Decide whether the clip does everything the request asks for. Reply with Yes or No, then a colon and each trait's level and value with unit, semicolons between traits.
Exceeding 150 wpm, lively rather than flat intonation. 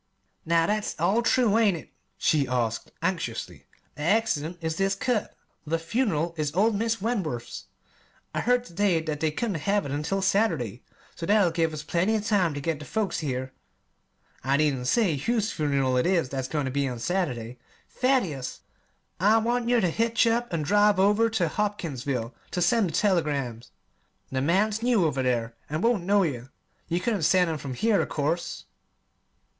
Yes: average, 180 wpm; wide, 6.5 semitones